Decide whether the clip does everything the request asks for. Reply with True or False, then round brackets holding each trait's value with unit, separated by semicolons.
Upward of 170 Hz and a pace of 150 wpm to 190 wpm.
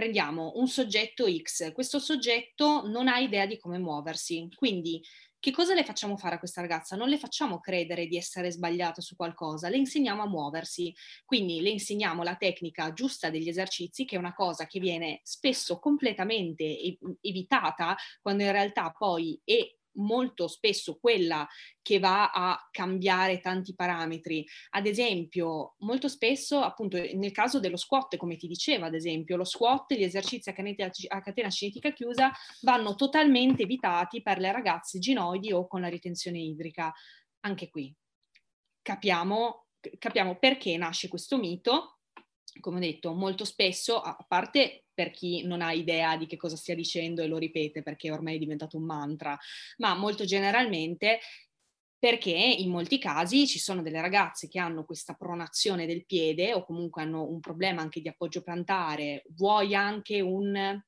True (185 Hz; 165 wpm)